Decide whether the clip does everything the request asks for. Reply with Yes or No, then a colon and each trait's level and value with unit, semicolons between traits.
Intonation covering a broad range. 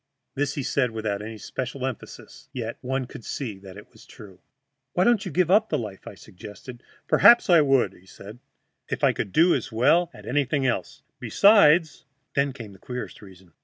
Yes: wide, 5.8 semitones